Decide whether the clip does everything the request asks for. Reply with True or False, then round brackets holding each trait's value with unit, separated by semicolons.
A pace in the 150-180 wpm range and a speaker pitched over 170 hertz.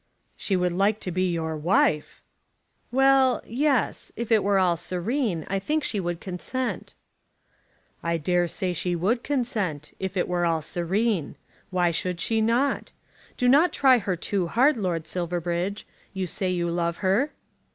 True (160 wpm; 185 Hz)